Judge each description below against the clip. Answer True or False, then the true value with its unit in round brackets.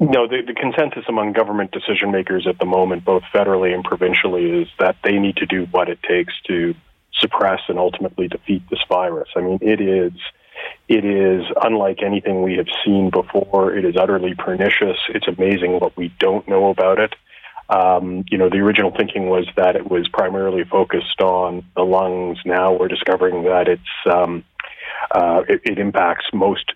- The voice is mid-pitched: False (95 Hz)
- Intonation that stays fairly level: True (1.5 semitones)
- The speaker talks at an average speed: True (180 wpm)